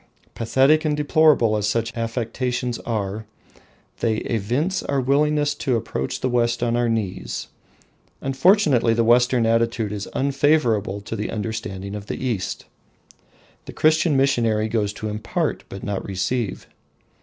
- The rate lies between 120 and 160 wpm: Yes, average, 140 wpm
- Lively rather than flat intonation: No, average, 3.9 semitones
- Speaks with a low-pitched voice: Yes, low, 115 Hz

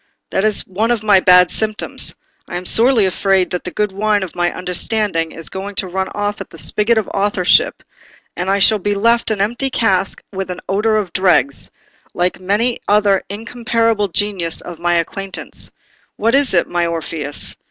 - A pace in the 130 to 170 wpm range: No, average, 185 wpm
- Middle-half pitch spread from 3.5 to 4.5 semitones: No, average, 3.0 semitones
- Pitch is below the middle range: No, high, 195 Hz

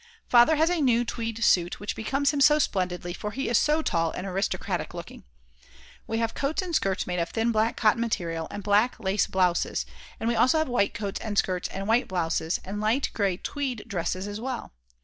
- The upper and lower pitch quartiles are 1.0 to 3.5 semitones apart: No, average, 4.6 semitones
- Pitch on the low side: No, high, 215 Hz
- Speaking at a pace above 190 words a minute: Yes, fast, 205 wpm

